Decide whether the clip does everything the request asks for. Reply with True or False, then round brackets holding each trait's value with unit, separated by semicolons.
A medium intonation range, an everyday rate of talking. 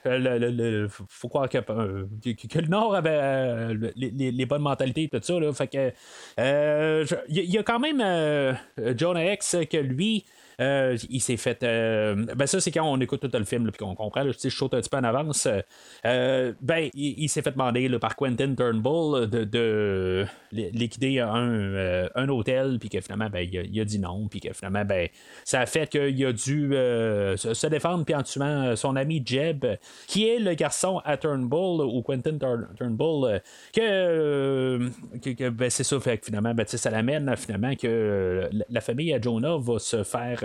True (4.5 semitones; 205 wpm)